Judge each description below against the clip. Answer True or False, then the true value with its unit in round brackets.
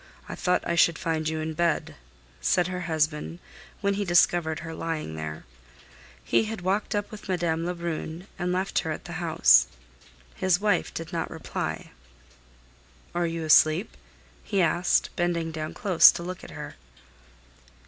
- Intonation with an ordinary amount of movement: False (2.2 semitones)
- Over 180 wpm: False (160 wpm)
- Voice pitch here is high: False (170 Hz)